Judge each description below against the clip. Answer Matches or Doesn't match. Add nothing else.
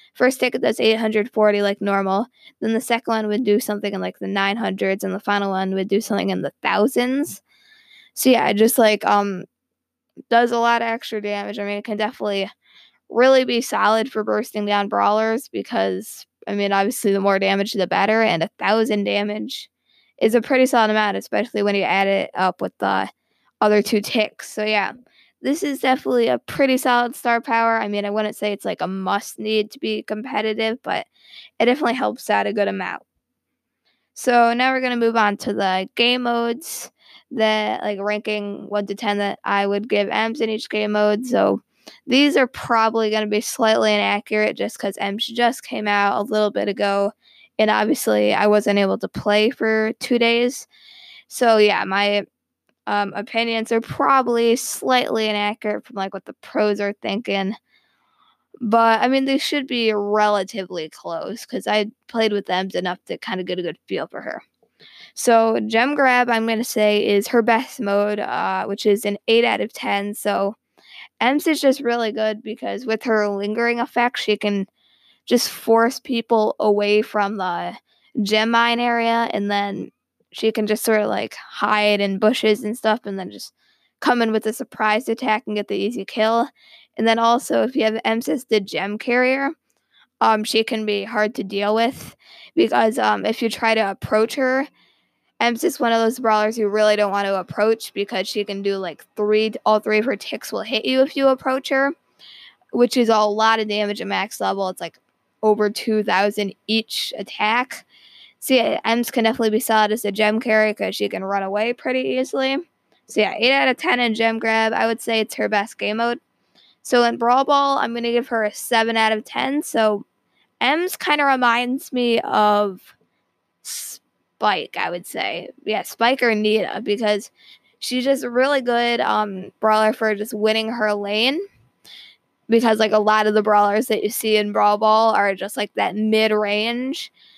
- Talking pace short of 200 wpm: Matches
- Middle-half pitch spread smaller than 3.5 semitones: Matches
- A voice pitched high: Matches